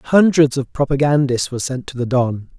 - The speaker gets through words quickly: No, average, 185 wpm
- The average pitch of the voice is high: No, low, 135 Hz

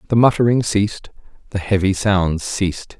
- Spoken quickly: No, average, 140 wpm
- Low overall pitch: Yes, low, 100 Hz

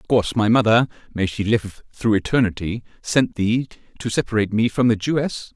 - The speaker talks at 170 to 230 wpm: No, average, 160 wpm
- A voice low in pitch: Yes, low, 110 Hz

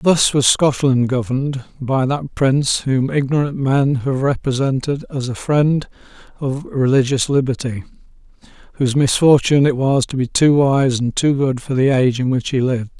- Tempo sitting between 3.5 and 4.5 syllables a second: No, 4.9 syllables/s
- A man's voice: Yes, male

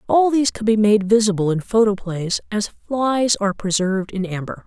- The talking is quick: No, average, 180 wpm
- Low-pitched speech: No, high, 210 Hz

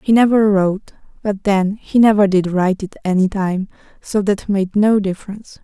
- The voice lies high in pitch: Yes, high, 200 Hz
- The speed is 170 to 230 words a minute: Yes, average, 180 wpm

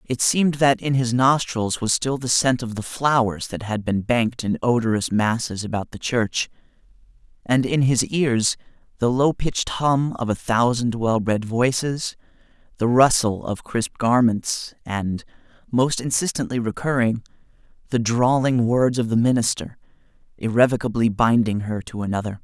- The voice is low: Yes, low, 120 Hz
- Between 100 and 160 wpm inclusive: Yes, average, 150 wpm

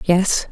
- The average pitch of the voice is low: No, medium, 180 Hz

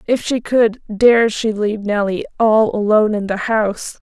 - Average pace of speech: Yes, average, 175 wpm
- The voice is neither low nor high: No, high, 215 Hz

